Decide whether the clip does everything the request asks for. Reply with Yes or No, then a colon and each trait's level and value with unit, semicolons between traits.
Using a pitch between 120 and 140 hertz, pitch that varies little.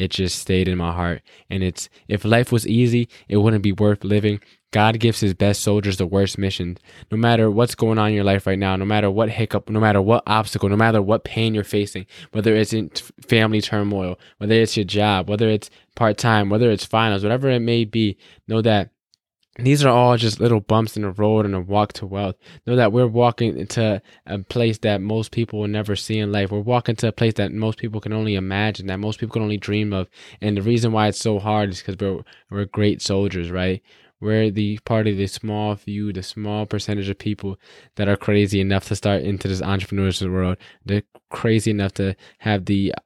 No: low, 105 Hz; narrow, 2.0 semitones